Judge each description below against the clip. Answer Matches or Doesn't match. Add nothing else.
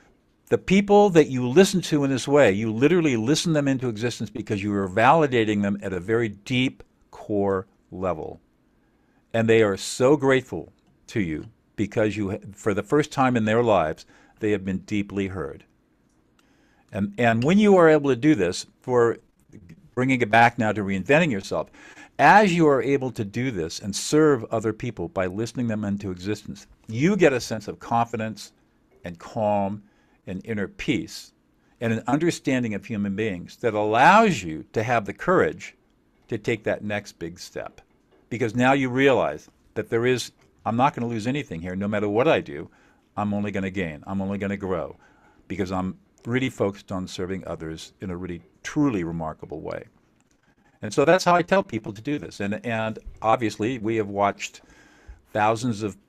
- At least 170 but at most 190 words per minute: Matches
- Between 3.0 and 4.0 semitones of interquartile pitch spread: Doesn't match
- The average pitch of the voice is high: Doesn't match